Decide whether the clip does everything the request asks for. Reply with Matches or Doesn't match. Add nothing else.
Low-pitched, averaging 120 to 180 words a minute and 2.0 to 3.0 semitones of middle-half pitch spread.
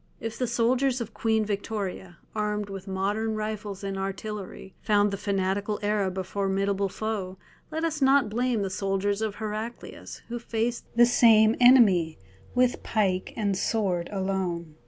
Doesn't match